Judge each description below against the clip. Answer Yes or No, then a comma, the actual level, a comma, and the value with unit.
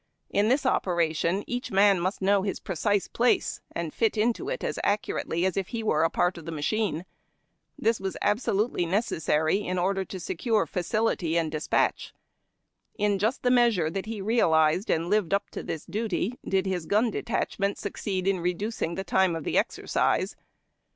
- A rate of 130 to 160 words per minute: No, average, 175 wpm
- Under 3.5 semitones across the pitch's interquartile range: No, average, 4.0 semitones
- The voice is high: Yes, high, 195 Hz